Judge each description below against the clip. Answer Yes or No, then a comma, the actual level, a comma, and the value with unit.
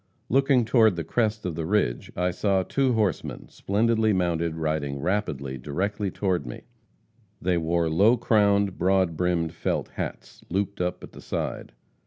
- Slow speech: No, average, 155 wpm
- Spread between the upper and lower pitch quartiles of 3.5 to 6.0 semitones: Yes, average, 4.2 semitones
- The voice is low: Yes, very low, 95 Hz